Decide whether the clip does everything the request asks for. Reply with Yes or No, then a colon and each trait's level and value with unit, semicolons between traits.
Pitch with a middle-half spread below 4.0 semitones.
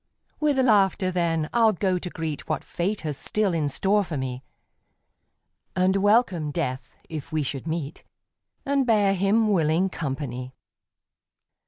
No: average, 5.2 semitones